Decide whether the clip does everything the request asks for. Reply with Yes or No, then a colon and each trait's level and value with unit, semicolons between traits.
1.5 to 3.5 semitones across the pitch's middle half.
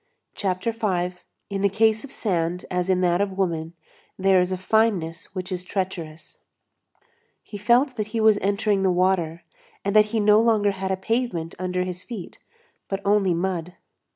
Yes: average, 2.7 semitones